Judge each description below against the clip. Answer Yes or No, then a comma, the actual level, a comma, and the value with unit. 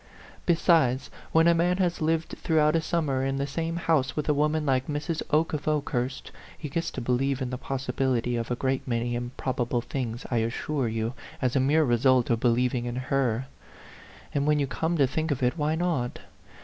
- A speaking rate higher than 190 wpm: Yes, average, 200 wpm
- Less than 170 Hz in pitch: Yes, low, 135 Hz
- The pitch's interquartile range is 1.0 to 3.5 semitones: No, average, 4.0 semitones